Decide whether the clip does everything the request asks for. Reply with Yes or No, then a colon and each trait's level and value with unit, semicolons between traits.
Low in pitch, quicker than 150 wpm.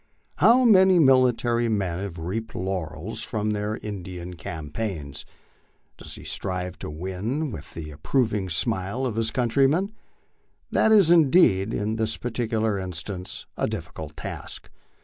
No: low, 105 Hz; slow, 135 wpm